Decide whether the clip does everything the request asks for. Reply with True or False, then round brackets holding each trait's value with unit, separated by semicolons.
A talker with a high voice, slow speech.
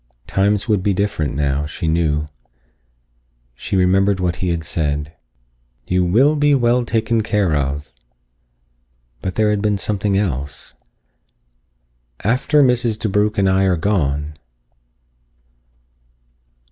False (95 Hz; 120 wpm)